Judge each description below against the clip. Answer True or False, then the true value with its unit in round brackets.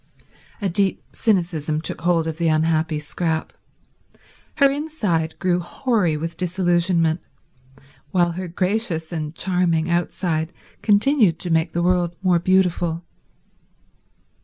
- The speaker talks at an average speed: False (115 wpm)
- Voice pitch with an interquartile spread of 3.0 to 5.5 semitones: False (2.4 semitones)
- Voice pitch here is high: False (175 Hz)